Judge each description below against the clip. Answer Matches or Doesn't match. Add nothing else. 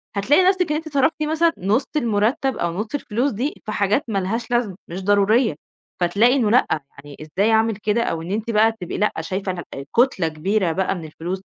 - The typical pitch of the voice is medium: Doesn't match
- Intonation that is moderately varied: Matches